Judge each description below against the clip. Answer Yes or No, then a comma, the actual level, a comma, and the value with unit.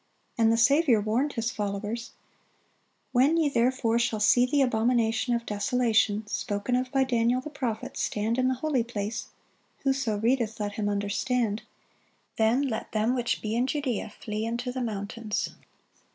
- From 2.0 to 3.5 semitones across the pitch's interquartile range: Yes, average, 2.8 semitones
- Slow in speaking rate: No, average, 155 wpm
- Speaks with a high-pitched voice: Yes, high, 230 Hz